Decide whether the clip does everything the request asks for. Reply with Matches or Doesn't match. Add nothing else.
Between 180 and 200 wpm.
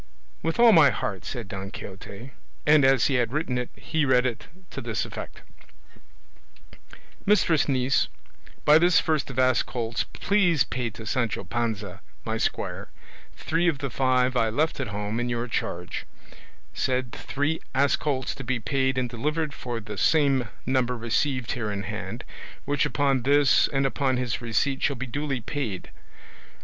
Doesn't match